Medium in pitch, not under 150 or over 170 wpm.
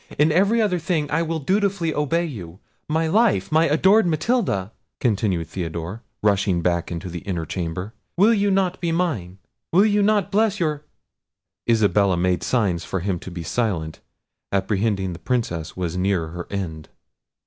No: low, 110 Hz; average, 160 wpm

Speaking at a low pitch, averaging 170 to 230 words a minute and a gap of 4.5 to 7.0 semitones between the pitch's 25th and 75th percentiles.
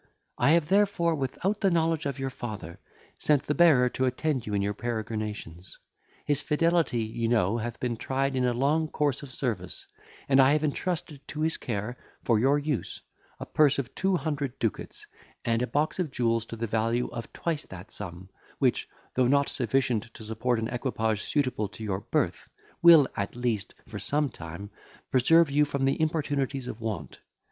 Yes: low, 130 Hz; average, 185 wpm; average, 4.8 semitones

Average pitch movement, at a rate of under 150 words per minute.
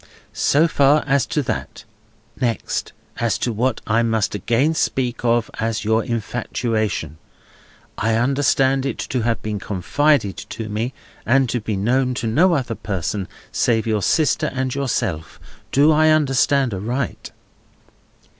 Yes: average, 3.7 semitones; average, 140 wpm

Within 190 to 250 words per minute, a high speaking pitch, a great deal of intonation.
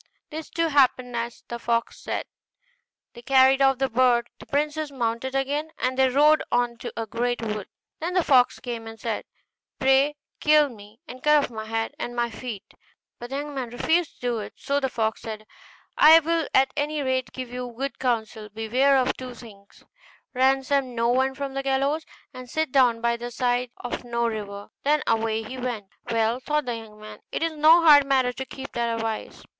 No: average, 200 wpm; very high, 255 Hz; average, 3.1 semitones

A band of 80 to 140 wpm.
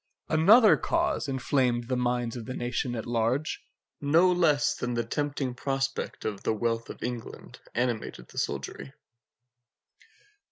Yes: slow, 135 wpm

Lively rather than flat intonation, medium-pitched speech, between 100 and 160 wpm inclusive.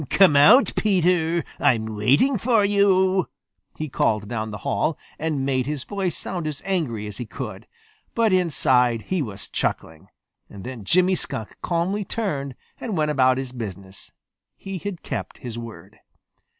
Yes: wide, 8.1 semitones; medium, 150 Hz; average, 150 wpm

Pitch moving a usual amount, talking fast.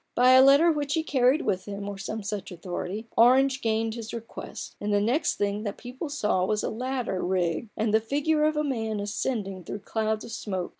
Yes: average, 4.4 semitones; fast, 215 wpm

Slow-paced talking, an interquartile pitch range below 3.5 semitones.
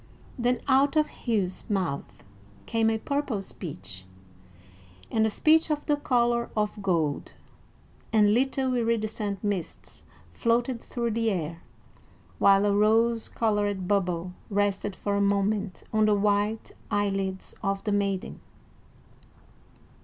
Yes: slow, 125 wpm; average, 2.9 semitones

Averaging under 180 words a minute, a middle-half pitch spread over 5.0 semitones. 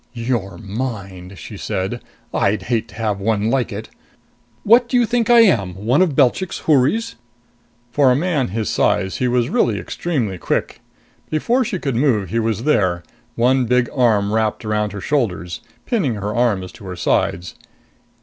Yes: average, 170 wpm; wide, 5.6 semitones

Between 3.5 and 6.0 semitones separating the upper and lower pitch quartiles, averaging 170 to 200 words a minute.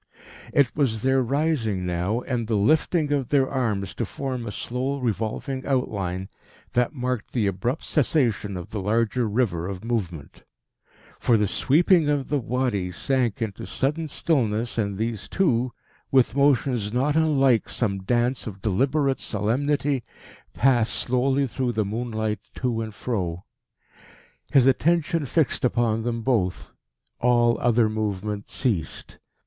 No: average, 4.2 semitones; average, 140 wpm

